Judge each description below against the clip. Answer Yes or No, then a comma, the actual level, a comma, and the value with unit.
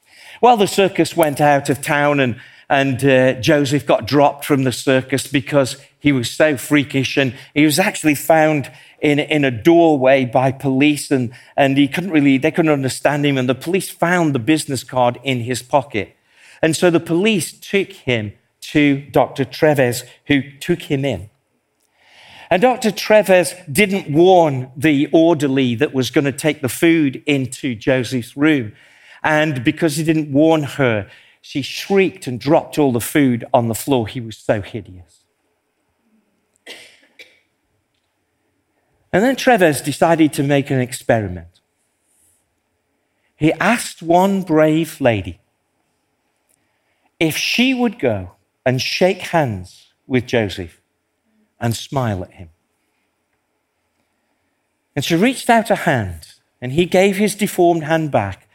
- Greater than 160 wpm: No, average, 145 wpm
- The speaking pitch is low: No, medium, 145 Hz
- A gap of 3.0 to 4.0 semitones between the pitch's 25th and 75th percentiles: No, average, 4.4 semitones